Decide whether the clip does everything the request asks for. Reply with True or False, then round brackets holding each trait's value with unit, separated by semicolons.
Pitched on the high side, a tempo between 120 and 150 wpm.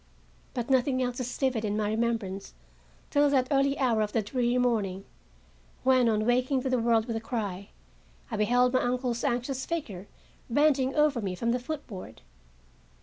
False (245 Hz; 175 wpm)